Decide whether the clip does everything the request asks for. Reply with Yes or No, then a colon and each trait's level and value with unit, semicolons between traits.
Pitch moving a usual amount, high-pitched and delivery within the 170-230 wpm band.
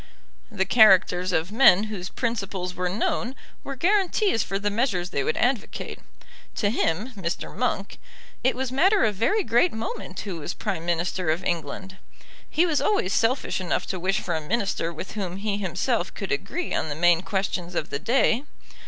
Yes: average, 5.0 semitones; high, 195 Hz; average, 180 wpm